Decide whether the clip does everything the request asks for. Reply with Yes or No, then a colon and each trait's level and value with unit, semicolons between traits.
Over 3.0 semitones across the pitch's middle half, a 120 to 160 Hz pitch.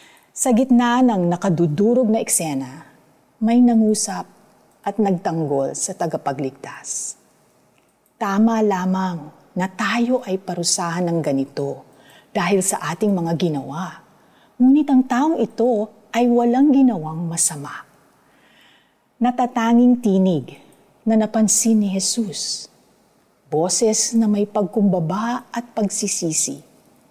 No: wide, 5.5 semitones; high, 205 Hz